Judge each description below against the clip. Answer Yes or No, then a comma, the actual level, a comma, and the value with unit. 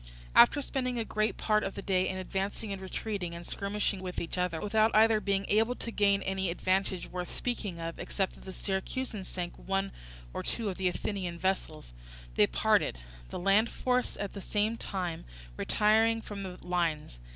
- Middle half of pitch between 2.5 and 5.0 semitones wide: Yes, average, 2.8 semitones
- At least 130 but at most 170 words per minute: No, average, 185 wpm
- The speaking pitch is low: No, high, 195 Hz